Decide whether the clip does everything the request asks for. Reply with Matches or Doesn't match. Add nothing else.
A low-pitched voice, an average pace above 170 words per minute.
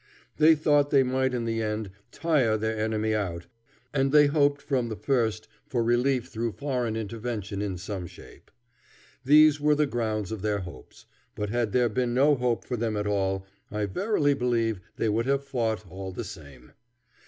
Matches